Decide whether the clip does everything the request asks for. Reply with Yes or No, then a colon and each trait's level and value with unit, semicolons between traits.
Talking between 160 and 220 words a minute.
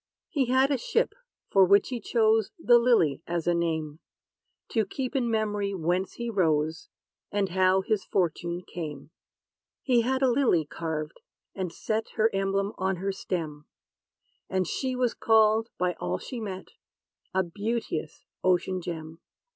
No: average, 150 wpm